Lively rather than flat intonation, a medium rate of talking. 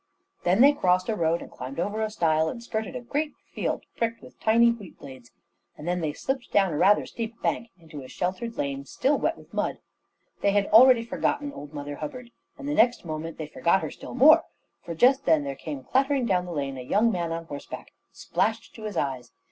No: wide, 7.1 semitones; fast, 220 wpm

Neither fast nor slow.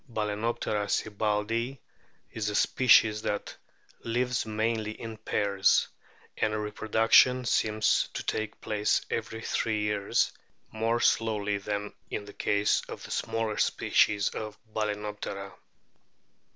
No: slow, 110 wpm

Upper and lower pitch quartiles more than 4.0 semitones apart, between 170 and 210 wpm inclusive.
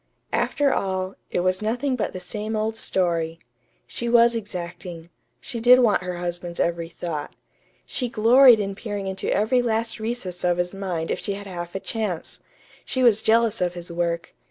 Yes: average, 4.5 semitones; average, 180 wpm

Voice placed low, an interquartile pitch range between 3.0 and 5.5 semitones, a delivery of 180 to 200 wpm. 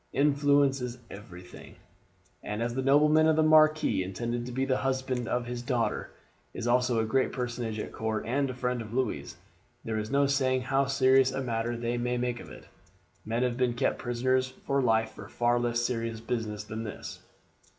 No: low, 125 Hz; narrow, 2.5 semitones; average, 190 wpm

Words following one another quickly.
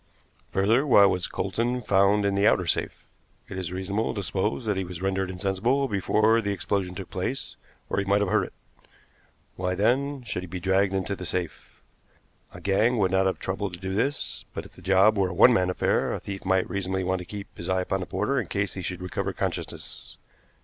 Yes: fast, 220 wpm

